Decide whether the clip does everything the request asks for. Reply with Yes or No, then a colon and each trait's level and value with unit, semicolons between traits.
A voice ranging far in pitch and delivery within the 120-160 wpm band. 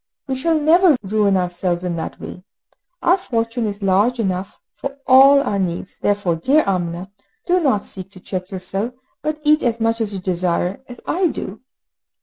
No: wide, 6.4 semitones; average, 175 wpm